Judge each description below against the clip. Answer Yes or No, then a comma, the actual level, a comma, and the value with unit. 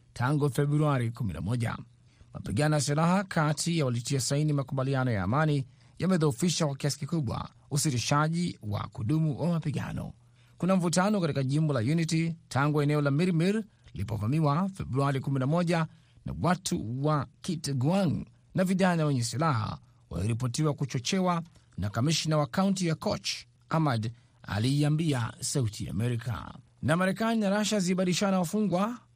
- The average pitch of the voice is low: No, medium, 150 Hz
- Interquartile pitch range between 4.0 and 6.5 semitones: Yes, average, 5.2 semitones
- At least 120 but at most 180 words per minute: Yes, average, 125 wpm